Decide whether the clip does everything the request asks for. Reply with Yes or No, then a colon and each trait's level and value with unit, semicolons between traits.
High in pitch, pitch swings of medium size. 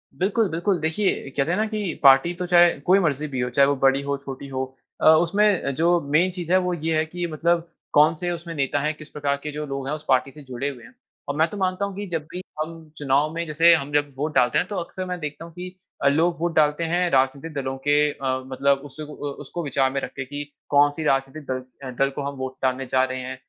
No: medium, 150 Hz; average, 3.9 semitones